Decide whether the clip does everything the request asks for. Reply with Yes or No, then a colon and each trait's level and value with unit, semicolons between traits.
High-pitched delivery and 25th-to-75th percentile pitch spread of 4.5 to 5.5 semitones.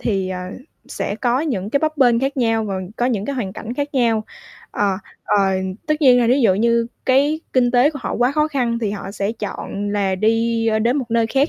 No: high, 235 Hz; average, 4.1 semitones